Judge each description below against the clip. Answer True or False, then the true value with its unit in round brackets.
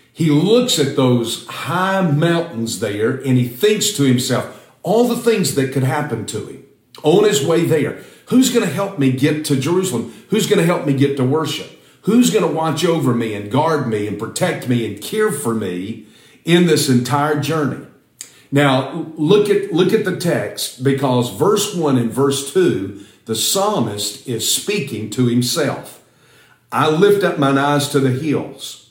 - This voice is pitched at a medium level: True (145 Hz)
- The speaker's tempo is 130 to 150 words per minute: False (180 wpm)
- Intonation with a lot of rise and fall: True (6.4 semitones)